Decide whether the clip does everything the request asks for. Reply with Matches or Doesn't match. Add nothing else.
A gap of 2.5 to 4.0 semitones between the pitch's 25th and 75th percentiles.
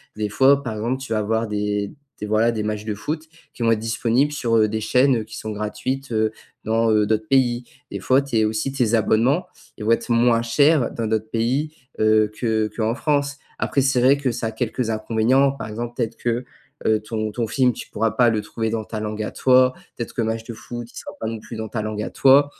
Matches